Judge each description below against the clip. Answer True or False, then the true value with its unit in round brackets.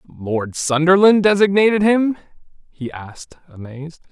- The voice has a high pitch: False (170 Hz)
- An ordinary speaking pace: False (100 wpm)